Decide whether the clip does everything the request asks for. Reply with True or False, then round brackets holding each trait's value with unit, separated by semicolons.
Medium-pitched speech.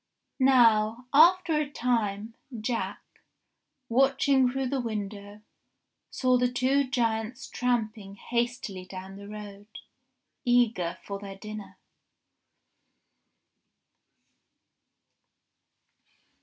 False (230 Hz)